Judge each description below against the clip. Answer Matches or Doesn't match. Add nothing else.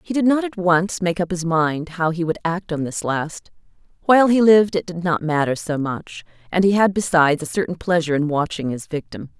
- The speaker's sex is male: Doesn't match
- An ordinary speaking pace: Doesn't match